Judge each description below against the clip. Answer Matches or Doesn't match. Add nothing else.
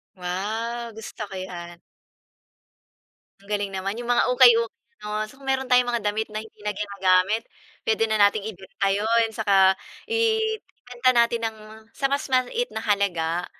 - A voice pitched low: Doesn't match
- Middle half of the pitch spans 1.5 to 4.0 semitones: Matches